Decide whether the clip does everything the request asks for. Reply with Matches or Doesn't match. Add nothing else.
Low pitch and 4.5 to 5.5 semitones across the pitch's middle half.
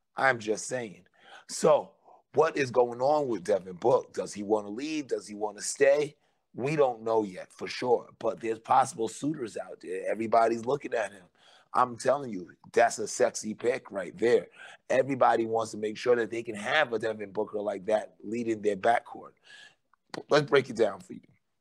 Matches